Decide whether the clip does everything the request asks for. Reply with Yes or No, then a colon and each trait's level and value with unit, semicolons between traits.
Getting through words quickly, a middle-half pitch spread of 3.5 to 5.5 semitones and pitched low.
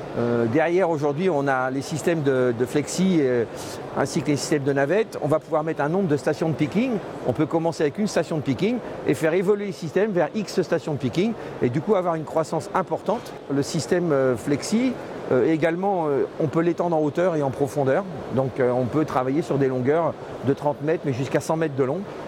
No: fast, 225 wpm; average, 4.2 semitones; medium, 155 Hz